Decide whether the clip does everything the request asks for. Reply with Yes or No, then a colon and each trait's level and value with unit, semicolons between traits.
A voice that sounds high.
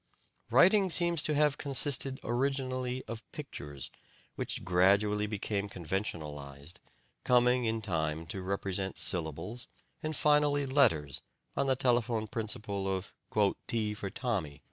No: low, 110 Hz